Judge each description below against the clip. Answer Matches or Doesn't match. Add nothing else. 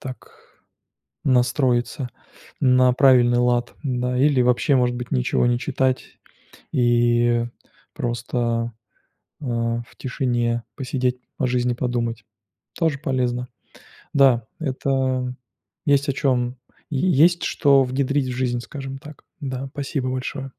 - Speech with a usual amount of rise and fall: Doesn't match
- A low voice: Matches